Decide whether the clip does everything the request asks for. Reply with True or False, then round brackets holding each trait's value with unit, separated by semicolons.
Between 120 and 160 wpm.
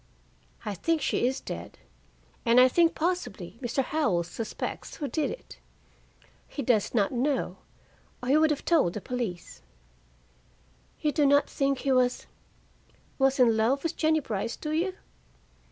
True (155 wpm)